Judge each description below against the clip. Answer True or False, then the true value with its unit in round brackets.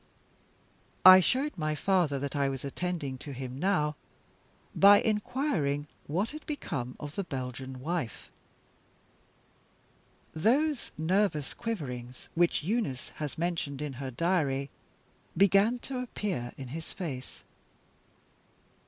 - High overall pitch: False (155 Hz)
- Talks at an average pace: False (115 wpm)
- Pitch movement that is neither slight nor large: False (6.5 semitones)